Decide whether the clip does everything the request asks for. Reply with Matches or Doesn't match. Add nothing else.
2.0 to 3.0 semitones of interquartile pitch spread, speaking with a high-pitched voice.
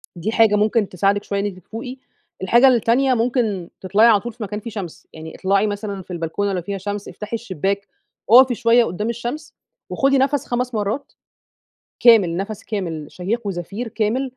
Doesn't match